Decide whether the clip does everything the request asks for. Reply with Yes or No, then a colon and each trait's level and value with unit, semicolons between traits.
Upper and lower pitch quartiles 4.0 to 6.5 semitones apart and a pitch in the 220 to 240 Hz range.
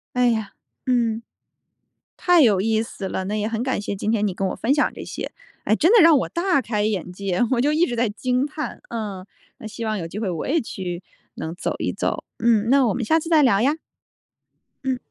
Yes: average, 4.5 semitones; high, 225 Hz